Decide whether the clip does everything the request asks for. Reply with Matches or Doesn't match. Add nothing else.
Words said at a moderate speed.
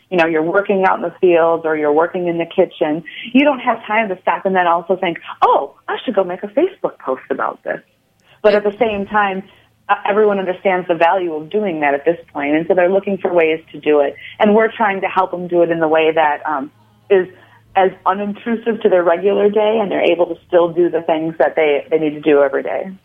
Doesn't match